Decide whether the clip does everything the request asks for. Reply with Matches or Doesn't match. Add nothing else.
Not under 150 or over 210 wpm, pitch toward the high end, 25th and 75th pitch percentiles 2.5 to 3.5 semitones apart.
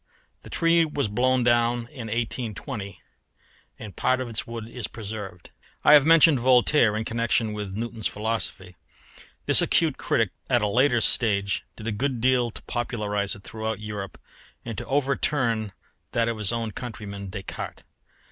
Doesn't match